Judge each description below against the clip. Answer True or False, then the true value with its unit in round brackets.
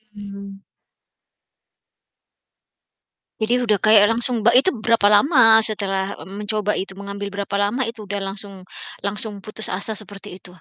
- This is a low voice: False (205 Hz)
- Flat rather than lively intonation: True (1.8 semitones)